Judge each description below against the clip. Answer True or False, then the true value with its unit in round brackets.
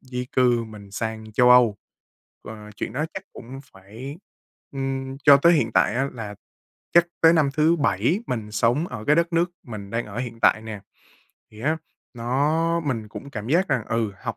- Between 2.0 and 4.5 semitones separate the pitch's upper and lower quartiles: False (5.1 semitones)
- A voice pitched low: True (125 Hz)